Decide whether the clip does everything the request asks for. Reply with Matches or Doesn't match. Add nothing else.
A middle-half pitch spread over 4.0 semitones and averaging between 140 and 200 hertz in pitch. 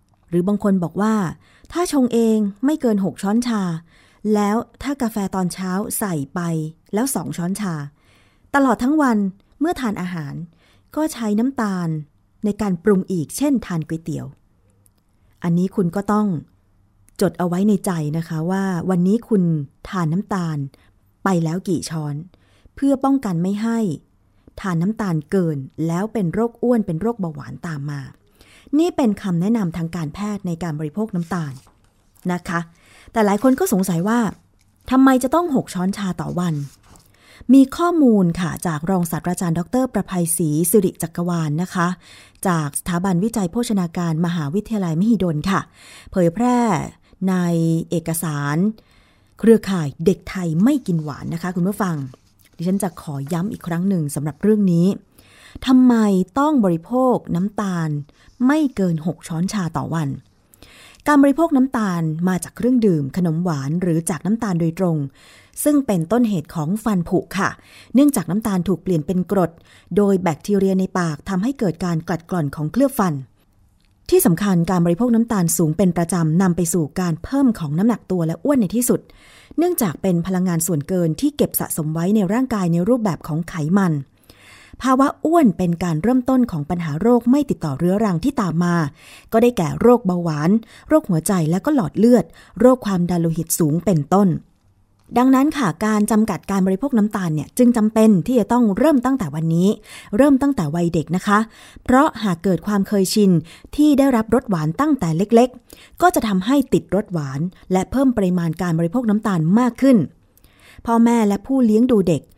Matches